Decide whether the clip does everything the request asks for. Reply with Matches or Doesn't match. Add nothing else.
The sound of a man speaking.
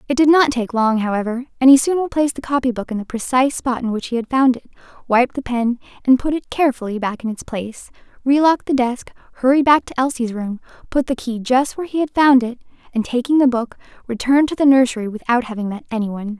Doesn't match